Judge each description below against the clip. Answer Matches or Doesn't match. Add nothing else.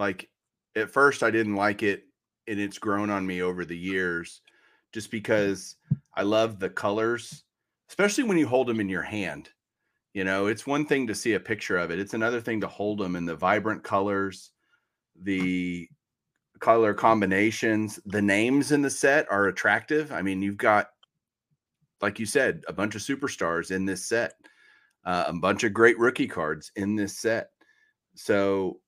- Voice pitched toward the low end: Matches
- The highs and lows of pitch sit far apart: Doesn't match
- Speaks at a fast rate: Doesn't match